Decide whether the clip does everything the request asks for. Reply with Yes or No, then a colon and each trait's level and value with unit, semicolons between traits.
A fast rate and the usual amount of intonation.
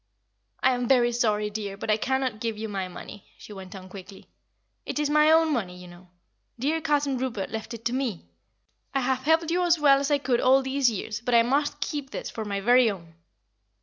Yes: fast, 220 wpm; average, 4.9 semitones